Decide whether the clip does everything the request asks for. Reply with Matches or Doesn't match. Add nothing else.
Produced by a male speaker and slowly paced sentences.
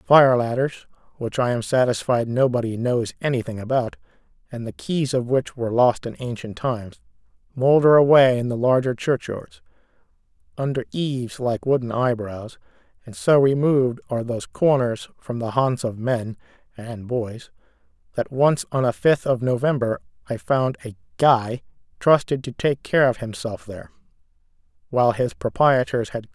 Doesn't match